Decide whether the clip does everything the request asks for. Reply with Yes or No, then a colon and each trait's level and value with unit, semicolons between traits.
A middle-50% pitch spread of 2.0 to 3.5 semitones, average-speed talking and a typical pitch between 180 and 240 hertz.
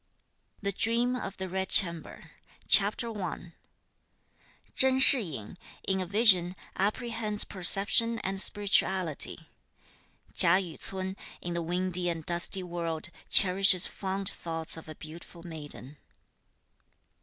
No: average, 2.9 semitones; slow, 120 wpm; medium, 185 Hz